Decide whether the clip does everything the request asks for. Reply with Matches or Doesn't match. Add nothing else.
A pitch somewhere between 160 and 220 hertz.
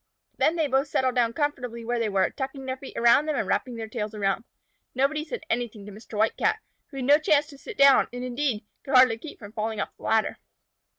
Doesn't match